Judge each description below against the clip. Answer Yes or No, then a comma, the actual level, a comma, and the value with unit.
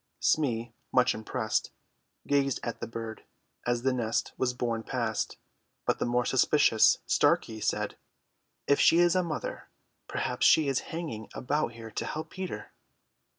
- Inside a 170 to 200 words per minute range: No, average, 150 wpm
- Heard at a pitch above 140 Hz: No, low, 125 Hz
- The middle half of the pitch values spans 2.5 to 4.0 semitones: No, average, 4.4 semitones